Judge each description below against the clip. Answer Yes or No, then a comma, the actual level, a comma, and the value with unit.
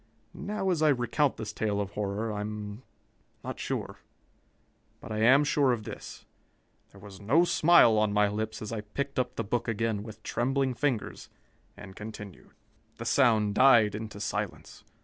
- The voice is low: Yes, low, 110 Hz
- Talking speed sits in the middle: Yes, average, 170 wpm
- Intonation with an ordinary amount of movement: Yes, average, 3.7 semitones